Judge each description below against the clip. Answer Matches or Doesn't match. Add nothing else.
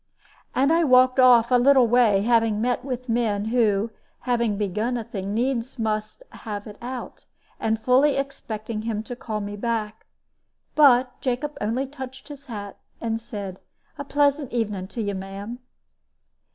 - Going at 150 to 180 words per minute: Matches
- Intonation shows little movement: Doesn't match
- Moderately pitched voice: Doesn't match